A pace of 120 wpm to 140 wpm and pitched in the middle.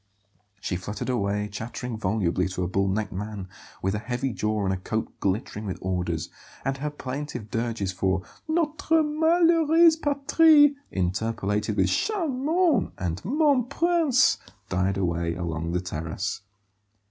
No: slow, 135 wpm; low, 110 Hz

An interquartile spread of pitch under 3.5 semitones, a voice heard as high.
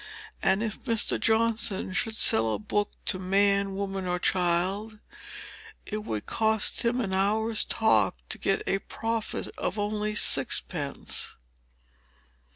Yes: narrow, 2.5 semitones; high, 205 Hz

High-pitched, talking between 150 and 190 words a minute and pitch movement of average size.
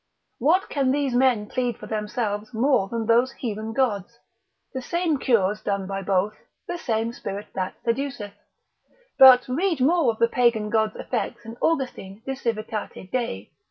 Yes: high, 230 Hz; average, 160 wpm; average, 3.8 semitones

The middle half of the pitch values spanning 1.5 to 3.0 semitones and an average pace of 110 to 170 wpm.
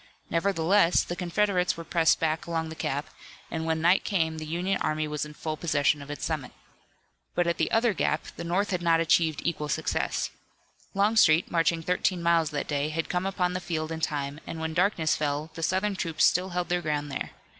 No: narrow, 2.4 semitones; fast, 205 wpm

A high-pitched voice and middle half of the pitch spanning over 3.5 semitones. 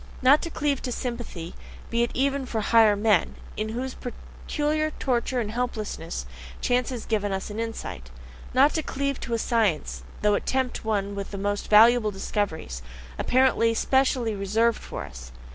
Yes: high, 230 Hz; average, 3.9 semitones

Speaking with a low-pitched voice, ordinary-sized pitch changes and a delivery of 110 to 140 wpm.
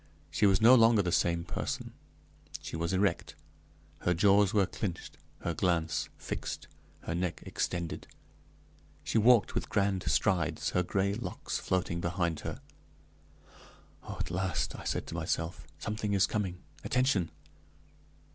Yes: very low, 95 Hz; average, 3.2 semitones; slow, 135 wpm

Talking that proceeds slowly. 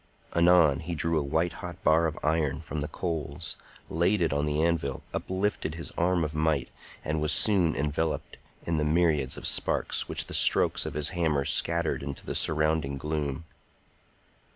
No: average, 175 wpm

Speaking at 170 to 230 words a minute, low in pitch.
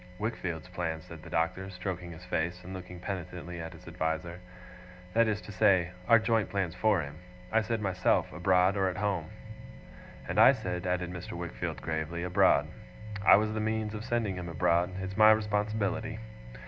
Yes: average, 175 wpm; very low, 90 Hz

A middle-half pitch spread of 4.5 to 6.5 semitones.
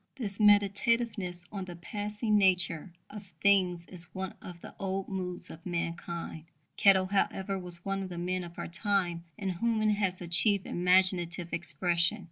No: narrow, 2.4 semitones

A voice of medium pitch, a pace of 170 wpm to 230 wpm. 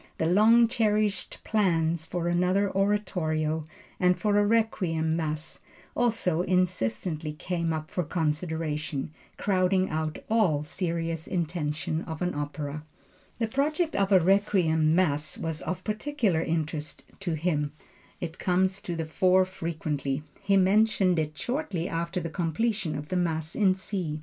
No: medium, 175 Hz; average, 140 wpm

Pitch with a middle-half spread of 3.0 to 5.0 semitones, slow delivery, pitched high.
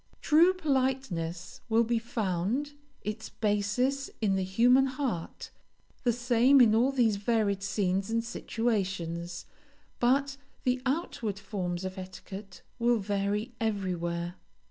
Yes: average, 4.6 semitones; slow, 120 wpm; high, 220 Hz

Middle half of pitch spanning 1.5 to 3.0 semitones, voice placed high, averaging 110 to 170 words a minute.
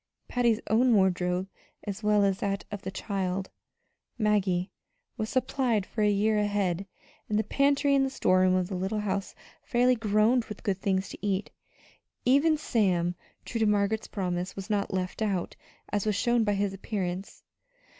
Yes: narrow, 2.6 semitones; high, 205 Hz; average, 165 wpm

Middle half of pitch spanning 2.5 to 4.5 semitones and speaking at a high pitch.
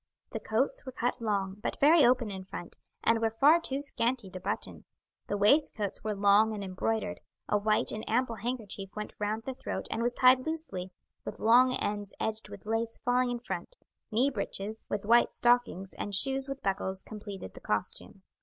Yes: average, 3.6 semitones; high, 225 Hz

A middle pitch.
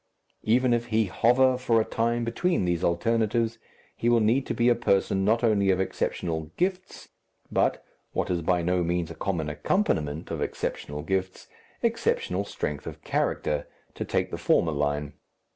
No: low, 100 Hz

